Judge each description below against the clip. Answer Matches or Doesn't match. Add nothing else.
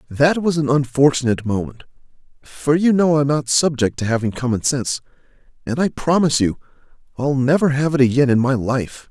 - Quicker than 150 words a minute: Matches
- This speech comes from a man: Matches